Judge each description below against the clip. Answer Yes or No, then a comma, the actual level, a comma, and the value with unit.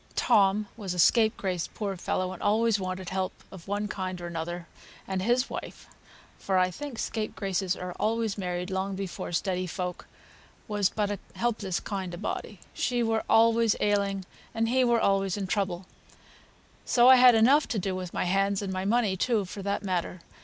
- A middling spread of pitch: Yes, average, 3.1 semitones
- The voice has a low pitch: No, high, 195 Hz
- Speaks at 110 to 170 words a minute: No, average, 180 wpm